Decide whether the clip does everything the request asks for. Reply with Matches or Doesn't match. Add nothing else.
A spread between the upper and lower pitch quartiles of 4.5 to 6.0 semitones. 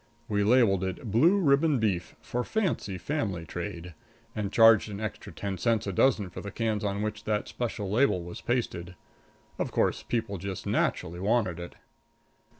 Doesn't match